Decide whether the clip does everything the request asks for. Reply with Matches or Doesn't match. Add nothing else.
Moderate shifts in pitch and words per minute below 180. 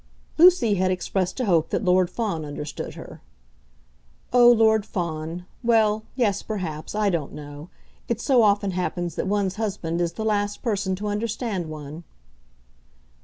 Matches